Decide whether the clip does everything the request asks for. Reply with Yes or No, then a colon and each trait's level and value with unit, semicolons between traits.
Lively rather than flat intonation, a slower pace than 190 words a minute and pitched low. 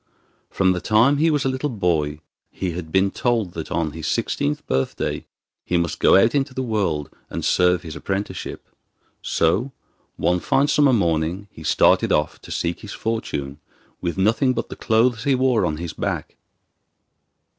Yes: wide, 6.6 semitones; average, 170 wpm; very low, 95 Hz